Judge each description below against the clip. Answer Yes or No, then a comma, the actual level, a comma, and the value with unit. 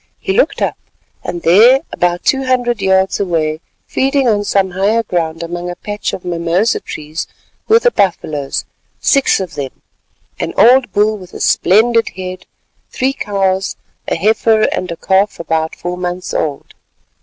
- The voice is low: No, high, 190 Hz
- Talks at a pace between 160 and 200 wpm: No, average, 150 wpm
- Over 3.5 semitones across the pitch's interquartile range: Yes, average, 4.4 semitones